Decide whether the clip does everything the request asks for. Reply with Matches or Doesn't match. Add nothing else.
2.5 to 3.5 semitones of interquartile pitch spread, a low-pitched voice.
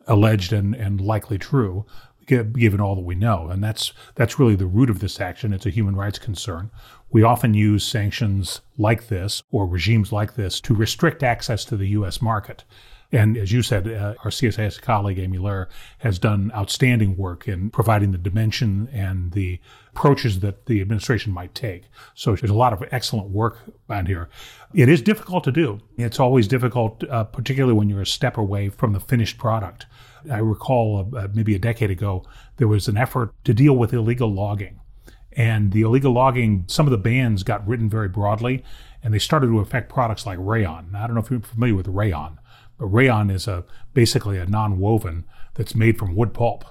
Matches